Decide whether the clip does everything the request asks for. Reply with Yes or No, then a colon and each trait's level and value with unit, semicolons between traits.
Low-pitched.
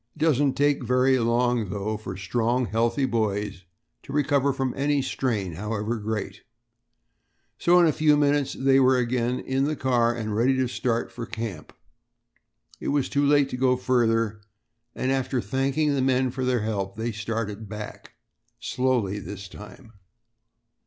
Yes: low, 125 Hz